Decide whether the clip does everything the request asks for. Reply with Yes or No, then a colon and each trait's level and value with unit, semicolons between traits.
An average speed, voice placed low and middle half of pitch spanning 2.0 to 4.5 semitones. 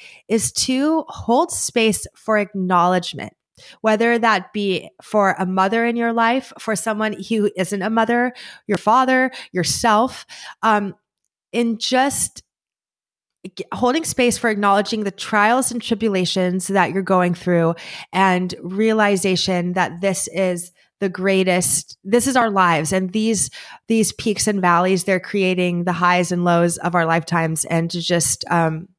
No: average, 145 wpm; high, 195 Hz; average, 4.0 semitones